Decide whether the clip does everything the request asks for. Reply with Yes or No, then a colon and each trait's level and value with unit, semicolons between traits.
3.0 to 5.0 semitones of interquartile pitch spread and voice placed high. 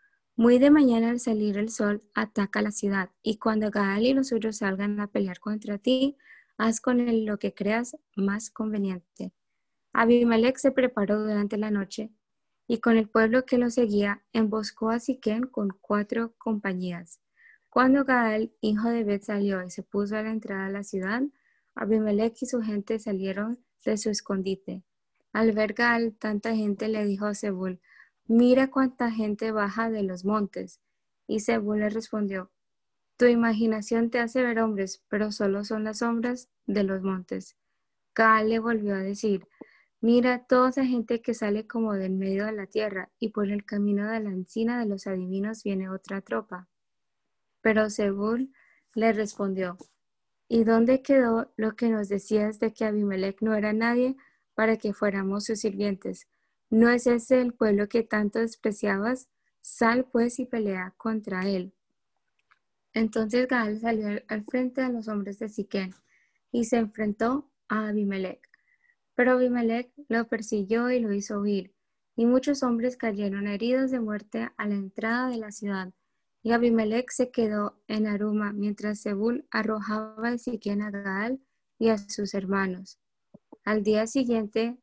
No: narrow, 2.5 semitones; high, 220 Hz